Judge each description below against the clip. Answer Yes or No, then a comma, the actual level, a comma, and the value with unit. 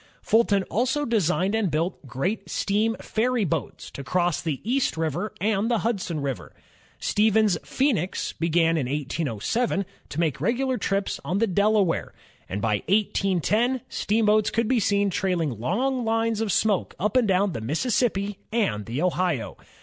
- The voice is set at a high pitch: Yes, high, 200 Hz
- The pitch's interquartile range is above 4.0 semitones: Yes, average, 5.3 semitones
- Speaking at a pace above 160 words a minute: No, average, 155 wpm